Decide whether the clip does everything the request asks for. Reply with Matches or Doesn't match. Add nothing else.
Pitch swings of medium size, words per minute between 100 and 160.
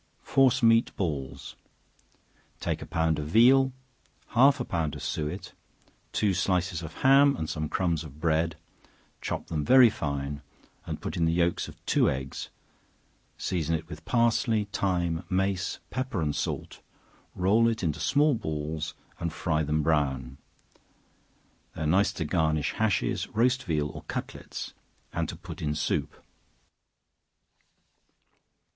Doesn't match